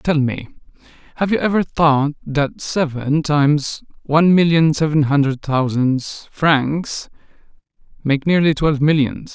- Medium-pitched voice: Yes, medium, 150 Hz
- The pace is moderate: No, slow, 120 wpm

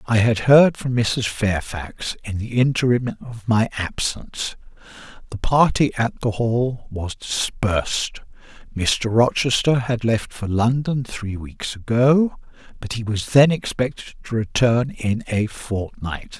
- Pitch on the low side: Yes, low, 115 Hz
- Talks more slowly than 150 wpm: Yes, average, 140 wpm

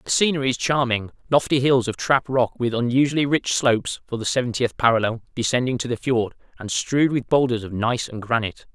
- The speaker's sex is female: No, male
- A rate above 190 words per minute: Yes, average, 200 wpm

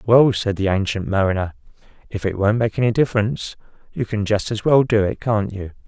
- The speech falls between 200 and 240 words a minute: Yes, fast, 205 wpm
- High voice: No, low, 105 Hz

